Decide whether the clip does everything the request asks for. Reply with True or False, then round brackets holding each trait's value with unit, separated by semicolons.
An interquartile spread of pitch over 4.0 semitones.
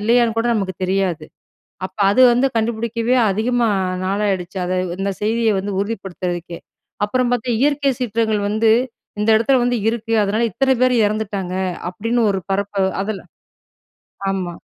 False (3.4 semitones)